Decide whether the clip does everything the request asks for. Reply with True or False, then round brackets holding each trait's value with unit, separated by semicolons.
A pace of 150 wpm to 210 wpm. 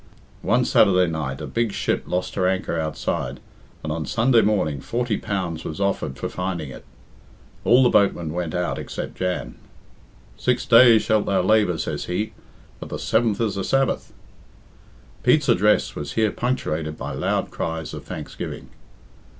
True (160 wpm)